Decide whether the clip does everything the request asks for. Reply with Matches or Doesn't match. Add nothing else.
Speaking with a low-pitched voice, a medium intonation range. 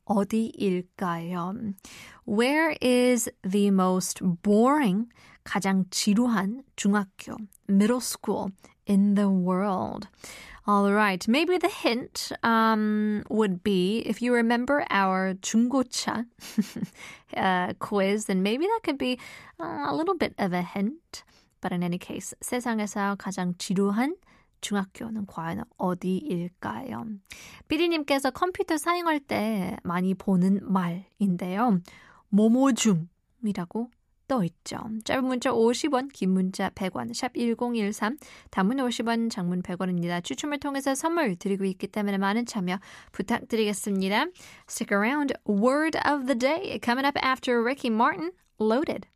Doesn't match